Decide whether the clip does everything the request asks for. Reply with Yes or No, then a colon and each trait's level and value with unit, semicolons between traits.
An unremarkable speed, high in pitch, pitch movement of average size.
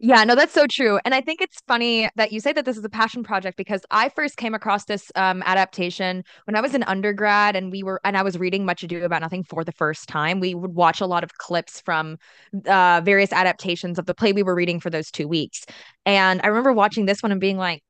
No: fast, 260 wpm; high, 195 Hz; average, 3.5 semitones